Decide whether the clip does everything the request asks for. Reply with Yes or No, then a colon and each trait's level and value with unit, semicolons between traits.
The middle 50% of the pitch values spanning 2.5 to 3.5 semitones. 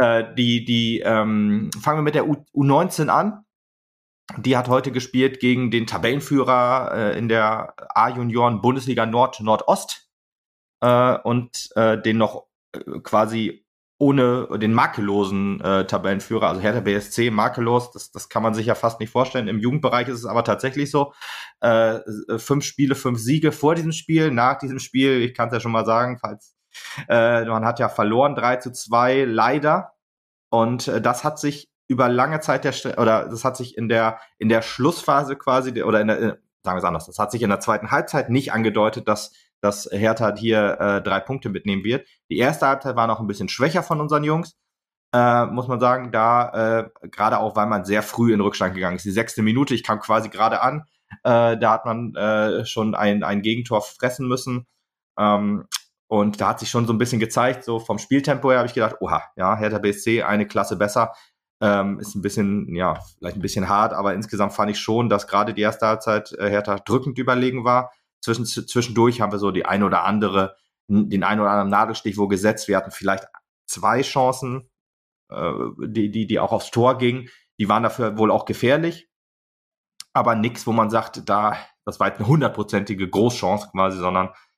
Yes: average, 3.2 semitones